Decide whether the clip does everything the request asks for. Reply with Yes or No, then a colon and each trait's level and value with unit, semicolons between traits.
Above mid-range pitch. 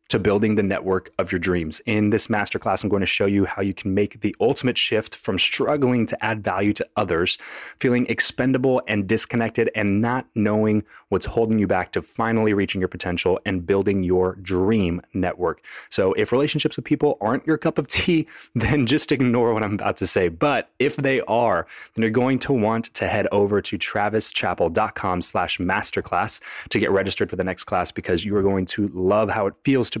No: low, 105 Hz